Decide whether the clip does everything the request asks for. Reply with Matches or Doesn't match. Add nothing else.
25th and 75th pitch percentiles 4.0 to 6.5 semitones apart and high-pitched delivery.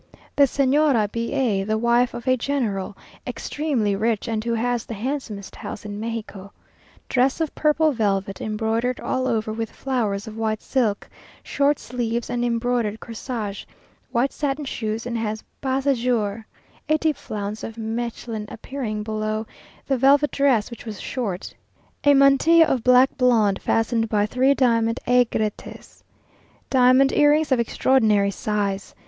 Doesn't match